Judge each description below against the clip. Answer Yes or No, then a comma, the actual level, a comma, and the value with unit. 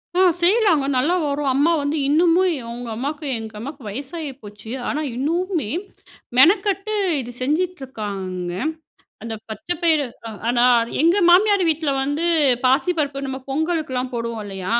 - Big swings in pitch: Yes, wide, 5.7 semitones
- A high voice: Yes, very high, 285 Hz